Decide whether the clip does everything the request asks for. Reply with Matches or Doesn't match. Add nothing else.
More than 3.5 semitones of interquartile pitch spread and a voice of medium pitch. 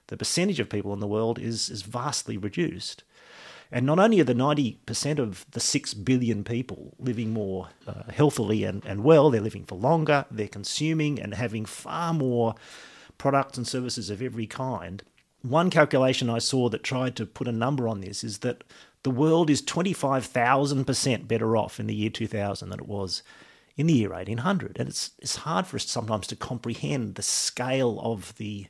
Doesn't match